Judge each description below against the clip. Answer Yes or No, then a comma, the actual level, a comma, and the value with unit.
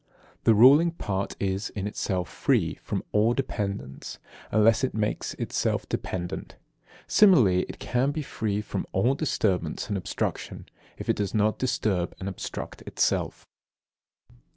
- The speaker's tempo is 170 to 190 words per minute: No, slow, 135 wpm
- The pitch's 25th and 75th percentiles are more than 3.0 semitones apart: Yes, average, 4.3 semitones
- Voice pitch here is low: Yes, low, 105 Hz